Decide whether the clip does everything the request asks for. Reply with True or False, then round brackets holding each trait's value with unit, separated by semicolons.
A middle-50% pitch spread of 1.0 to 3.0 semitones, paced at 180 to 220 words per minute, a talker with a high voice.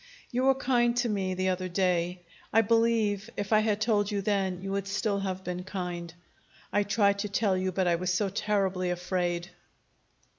True (2.5 semitones; 190 wpm; 195 Hz)